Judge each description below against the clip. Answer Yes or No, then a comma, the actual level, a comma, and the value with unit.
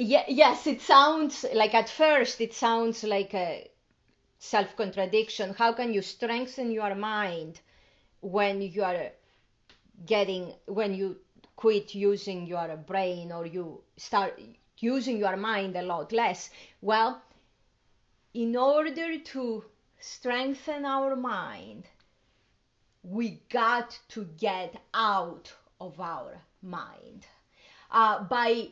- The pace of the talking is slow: Yes, slow, 110 wpm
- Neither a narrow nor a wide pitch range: Yes, average, 3.9 semitones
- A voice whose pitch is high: Yes, high, 225 Hz